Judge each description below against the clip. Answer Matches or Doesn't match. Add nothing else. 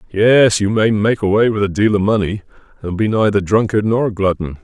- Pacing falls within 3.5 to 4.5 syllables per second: Doesn't match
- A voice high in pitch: Doesn't match